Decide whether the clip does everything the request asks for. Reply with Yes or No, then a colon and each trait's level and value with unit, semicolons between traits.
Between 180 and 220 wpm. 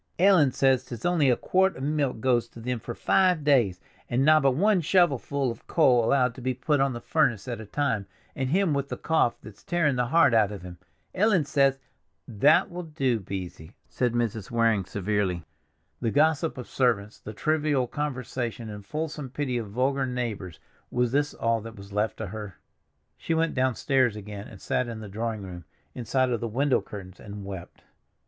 Yes: average, 190 wpm